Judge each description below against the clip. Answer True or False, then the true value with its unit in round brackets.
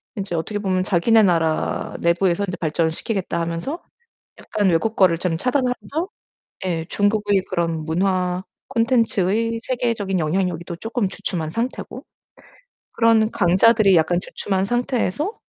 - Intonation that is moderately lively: True (4.8 semitones)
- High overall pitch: True (195 Hz)